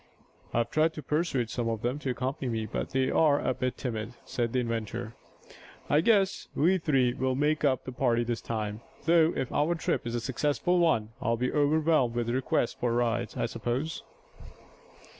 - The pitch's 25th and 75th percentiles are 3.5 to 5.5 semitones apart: Yes, average, 4.3 semitones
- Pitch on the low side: Yes, low, 125 Hz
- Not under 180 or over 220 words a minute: Yes, average, 185 wpm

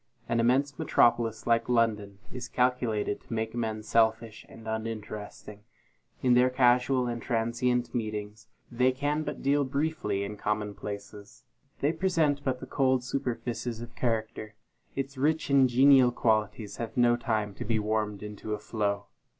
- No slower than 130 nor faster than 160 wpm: Yes, average, 150 wpm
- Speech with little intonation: No, average, 3.0 semitones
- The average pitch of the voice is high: No, low, 115 Hz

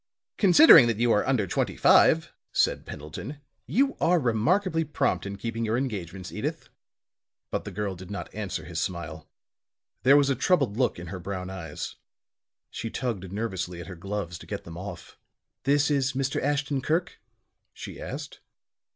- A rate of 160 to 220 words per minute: Yes, average, 165 wpm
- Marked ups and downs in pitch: Yes, wide, 6.9 semitones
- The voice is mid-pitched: No, low, 115 Hz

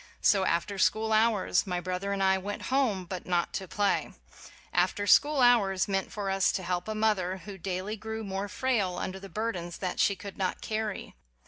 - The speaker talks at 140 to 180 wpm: No, average, 200 wpm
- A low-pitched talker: No, high, 195 Hz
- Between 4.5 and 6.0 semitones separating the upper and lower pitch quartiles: No, narrow, 2.5 semitones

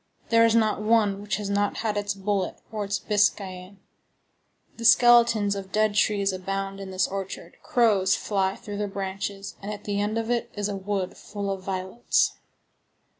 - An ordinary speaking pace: Yes, average, 175 wpm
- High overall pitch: Yes, high, 205 Hz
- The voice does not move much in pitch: Yes, narrow, 1.5 semitones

